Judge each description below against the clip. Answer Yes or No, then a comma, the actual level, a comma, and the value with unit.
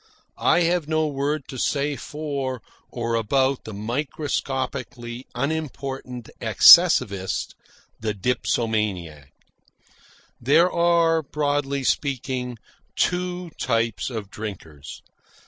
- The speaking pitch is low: Yes, low, 130 Hz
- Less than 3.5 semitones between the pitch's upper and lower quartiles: No, average, 4.5 semitones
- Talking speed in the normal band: No, slow, 90 wpm